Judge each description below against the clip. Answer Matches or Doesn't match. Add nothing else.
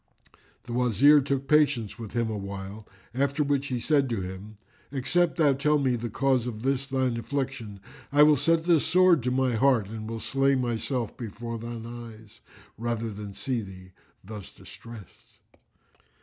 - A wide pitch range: Doesn't match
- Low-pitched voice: Matches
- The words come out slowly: Doesn't match